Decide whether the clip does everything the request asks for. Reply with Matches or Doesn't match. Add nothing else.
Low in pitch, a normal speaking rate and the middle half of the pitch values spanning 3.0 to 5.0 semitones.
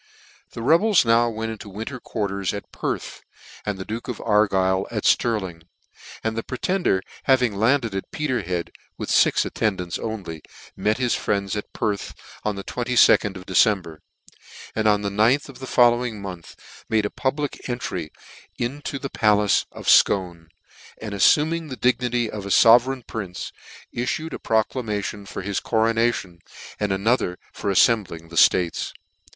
Matches